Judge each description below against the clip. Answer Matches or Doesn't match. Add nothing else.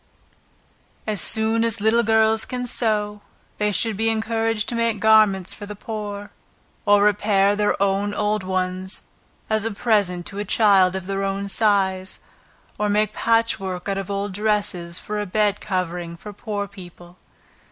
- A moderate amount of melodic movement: Doesn't match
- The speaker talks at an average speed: Matches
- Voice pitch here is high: Matches